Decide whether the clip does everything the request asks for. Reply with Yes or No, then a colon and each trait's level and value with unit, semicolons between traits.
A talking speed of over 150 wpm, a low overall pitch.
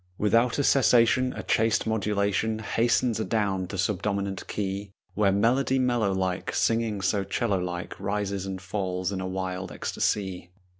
No: average, 145 wpm; low, 100 Hz